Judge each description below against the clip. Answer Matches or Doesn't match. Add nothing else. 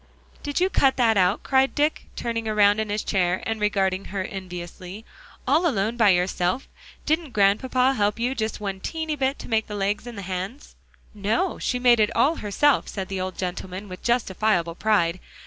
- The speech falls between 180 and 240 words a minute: Matches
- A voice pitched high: Matches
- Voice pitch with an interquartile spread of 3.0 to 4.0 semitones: Doesn't match